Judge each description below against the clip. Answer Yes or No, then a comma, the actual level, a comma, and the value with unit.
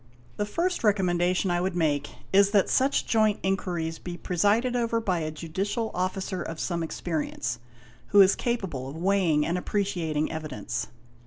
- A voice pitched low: No, medium, 185 Hz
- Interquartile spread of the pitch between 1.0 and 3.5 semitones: No, average, 3.9 semitones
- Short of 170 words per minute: Yes, average, 160 wpm